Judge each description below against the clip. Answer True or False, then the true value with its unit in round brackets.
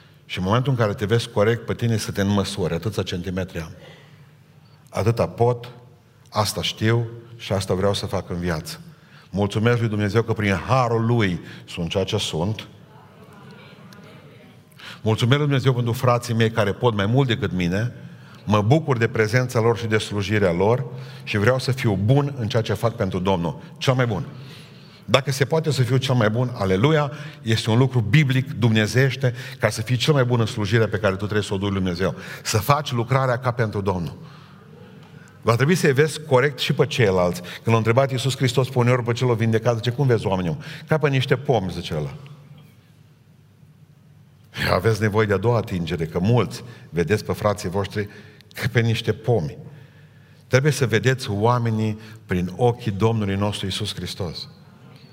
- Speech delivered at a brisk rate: True (175 wpm)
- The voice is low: True (120 Hz)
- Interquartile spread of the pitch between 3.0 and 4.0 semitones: False (4.4 semitones)